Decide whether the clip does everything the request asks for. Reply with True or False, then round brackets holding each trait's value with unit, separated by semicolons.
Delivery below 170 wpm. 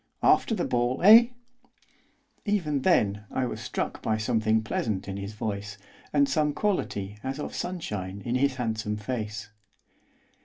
True (145 wpm)